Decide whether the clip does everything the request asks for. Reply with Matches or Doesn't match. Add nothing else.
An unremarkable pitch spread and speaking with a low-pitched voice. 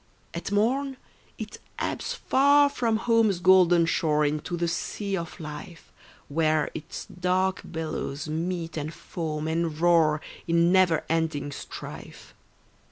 Doesn't match